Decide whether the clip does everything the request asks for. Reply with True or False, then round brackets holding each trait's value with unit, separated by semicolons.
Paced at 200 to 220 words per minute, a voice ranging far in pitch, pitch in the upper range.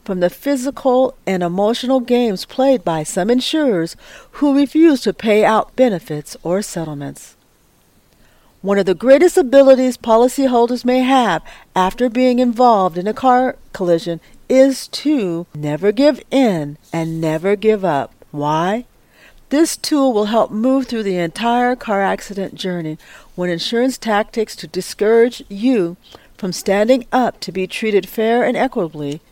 False (140 wpm; 5.8 semitones; 220 Hz)